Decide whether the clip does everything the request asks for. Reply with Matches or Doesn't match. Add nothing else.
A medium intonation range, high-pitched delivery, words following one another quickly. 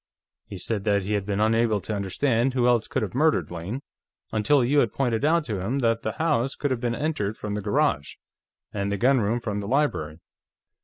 Doesn't match